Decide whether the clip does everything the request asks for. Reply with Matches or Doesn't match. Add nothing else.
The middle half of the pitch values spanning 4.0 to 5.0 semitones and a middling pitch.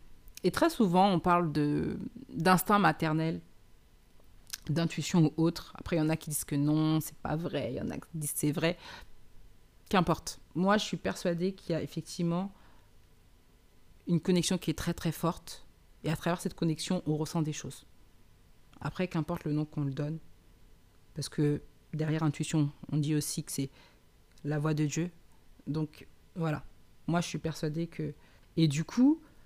Matches